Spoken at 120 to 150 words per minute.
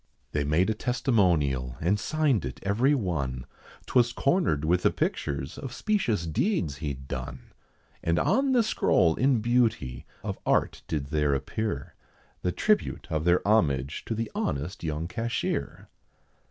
Yes: average, 145 wpm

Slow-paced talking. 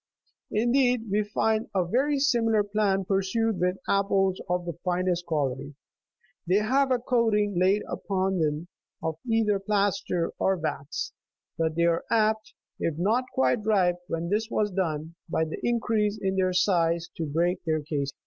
No: average, 160 wpm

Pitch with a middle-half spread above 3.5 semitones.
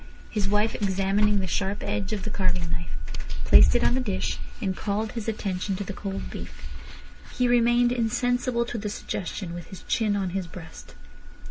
No: average, 3.1 semitones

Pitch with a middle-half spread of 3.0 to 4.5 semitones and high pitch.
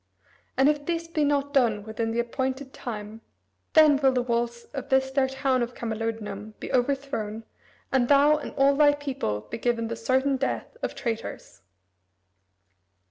Yes: average, 3.5 semitones; very high, 260 Hz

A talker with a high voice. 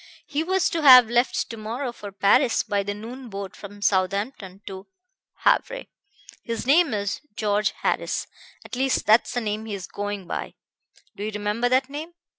Yes: high, 220 Hz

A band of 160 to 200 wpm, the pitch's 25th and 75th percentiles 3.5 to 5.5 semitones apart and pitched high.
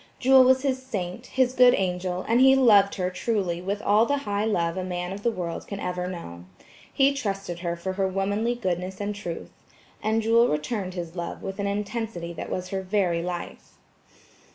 Yes: average, 195 wpm; average, 4.2 semitones; high, 195 Hz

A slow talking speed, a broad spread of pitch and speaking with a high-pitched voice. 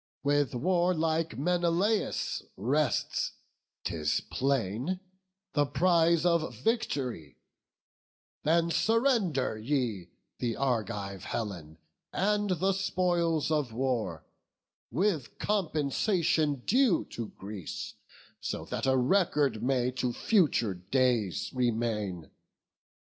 No: slow, 90 wpm; wide, 7.1 semitones; medium, 140 Hz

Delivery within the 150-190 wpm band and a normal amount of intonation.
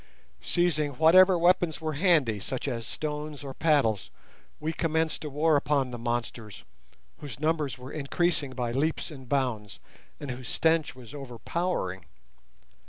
No: slow, 135 wpm; average, 4.5 semitones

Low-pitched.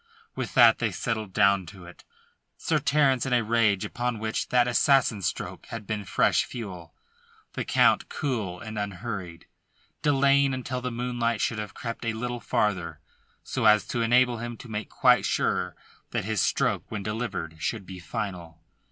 Yes: low, 110 Hz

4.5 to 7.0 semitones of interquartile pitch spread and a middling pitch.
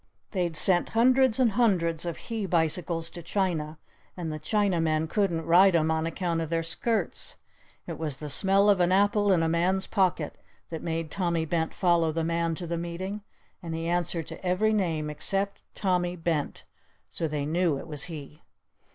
No: average, 2.8 semitones; medium, 170 Hz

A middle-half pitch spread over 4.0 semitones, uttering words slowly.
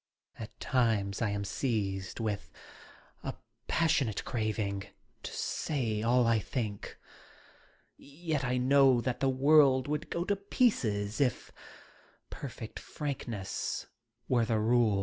Yes: average, 4.6 semitones; slow, 120 wpm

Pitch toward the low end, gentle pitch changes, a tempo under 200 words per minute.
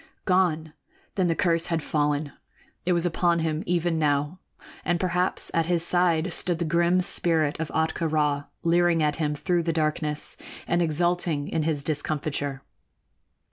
No: medium, 165 Hz; narrow, 2.3 semitones; average, 155 wpm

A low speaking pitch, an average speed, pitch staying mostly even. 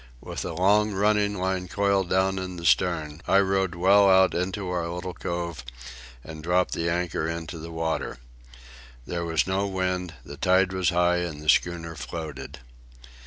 Yes: very low, 90 Hz; average, 165 wpm; narrow, 2.2 semitones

